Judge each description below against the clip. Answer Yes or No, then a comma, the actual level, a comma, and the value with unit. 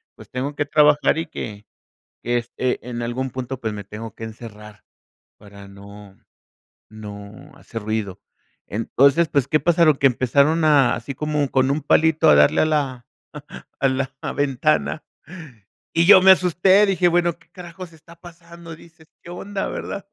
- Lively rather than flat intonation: Yes, wide, 6.5 semitones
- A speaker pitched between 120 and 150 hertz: Yes, medium, 140 Hz